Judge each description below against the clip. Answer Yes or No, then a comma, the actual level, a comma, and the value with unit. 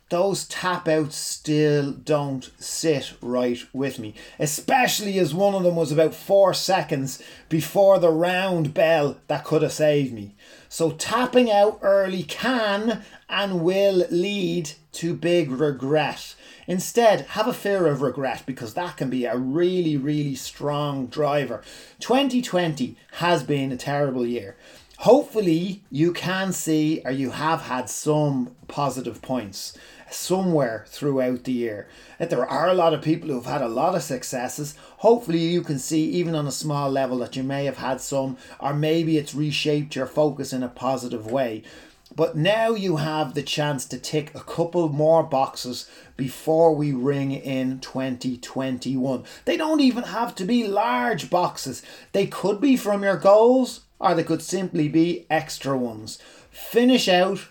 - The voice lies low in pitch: No, medium, 155 Hz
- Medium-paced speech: Yes, average, 160 wpm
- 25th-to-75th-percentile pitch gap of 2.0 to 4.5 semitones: No, average, 5.1 semitones